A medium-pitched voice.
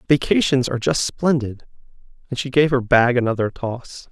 No: low, 130 Hz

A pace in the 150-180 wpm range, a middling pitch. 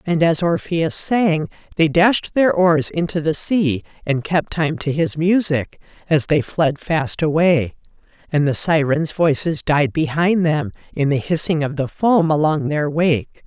Yes: average, 170 wpm; medium, 160 Hz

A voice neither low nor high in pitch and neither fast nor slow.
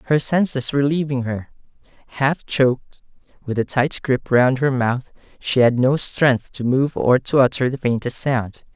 No: low, 130 Hz; average, 180 wpm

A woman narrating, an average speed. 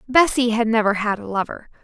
Yes: female; average, 195 wpm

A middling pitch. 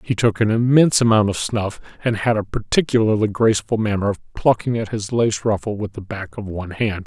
No: low, 105 Hz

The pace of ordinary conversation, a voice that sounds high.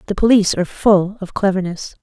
Yes: average, 180 wpm; high, 195 Hz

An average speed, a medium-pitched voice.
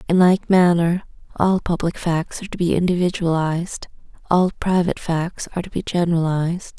Yes: average, 150 wpm; medium, 175 Hz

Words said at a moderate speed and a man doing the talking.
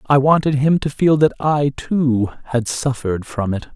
Yes: average, 190 wpm; male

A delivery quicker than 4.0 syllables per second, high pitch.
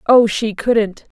No: 3.3 syllables/s; high, 220 Hz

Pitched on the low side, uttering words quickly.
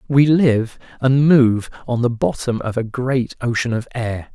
No: low, 125 Hz; average, 180 wpm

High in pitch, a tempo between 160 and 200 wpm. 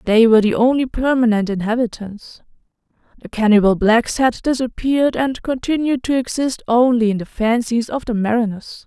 No: high, 235 Hz; average, 150 wpm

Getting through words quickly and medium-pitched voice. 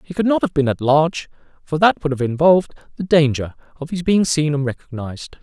Yes: fast, 220 wpm; medium, 150 Hz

